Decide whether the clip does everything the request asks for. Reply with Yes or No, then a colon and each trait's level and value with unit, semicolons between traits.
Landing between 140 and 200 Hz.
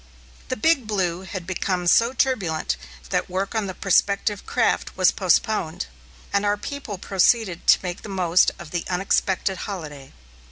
Yes: high, 190 Hz